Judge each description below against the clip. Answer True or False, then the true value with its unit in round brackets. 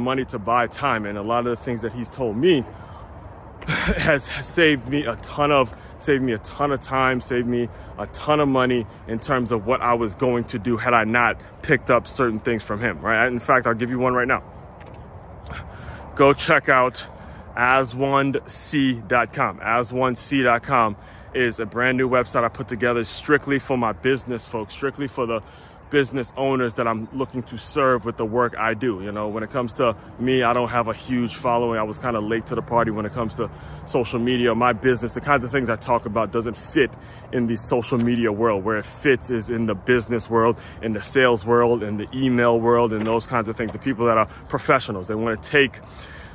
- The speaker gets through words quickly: True (215 wpm)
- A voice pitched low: True (120 Hz)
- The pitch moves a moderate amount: False (2.3 semitones)